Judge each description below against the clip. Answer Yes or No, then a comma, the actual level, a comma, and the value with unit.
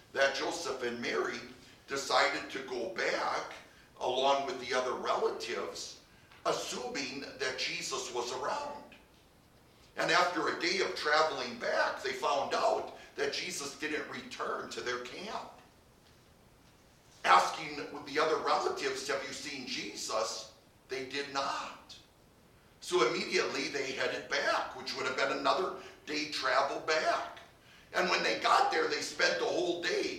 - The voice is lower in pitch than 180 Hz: Yes, medium, 140 Hz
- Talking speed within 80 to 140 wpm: Yes, slow, 135 wpm